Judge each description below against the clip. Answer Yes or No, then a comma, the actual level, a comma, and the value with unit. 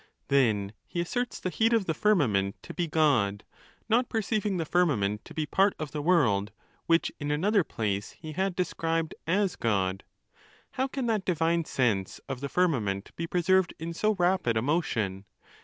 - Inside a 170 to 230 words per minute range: Yes, average, 175 wpm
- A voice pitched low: No, medium, 165 Hz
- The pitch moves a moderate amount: No, wide, 8.6 semitones